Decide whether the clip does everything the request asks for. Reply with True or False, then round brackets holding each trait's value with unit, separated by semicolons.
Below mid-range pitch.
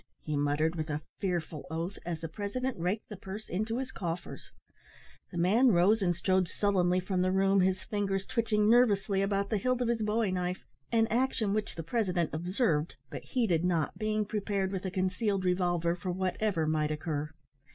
False (190 Hz)